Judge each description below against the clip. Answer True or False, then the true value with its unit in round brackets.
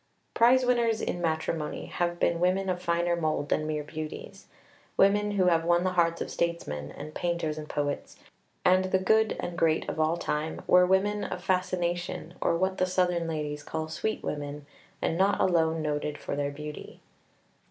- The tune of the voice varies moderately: True (3.1 semitones)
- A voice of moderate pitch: True (170 Hz)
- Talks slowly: False (175 wpm)